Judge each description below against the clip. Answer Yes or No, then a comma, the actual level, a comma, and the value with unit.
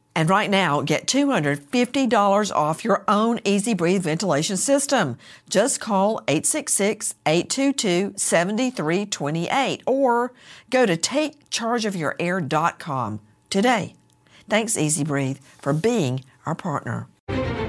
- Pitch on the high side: Yes, high, 195 Hz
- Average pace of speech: No, slow, 100 wpm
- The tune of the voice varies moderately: No, wide, 7.3 semitones